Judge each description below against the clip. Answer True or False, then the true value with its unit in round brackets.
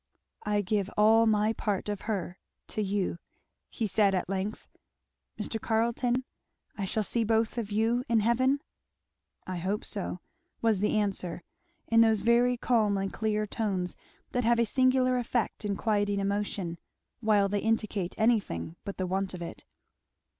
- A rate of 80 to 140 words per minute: False (155 wpm)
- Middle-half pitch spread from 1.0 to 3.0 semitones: True (2.5 semitones)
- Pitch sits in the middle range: False (210 Hz)